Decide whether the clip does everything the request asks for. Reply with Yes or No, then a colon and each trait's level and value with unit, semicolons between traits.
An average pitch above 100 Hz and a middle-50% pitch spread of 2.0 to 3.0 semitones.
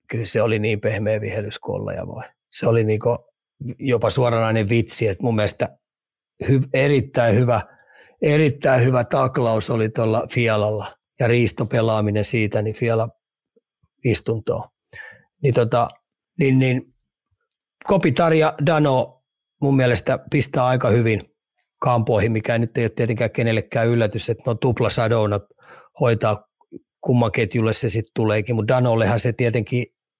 Yes: low, 115 Hz; narrow, 2.5 semitones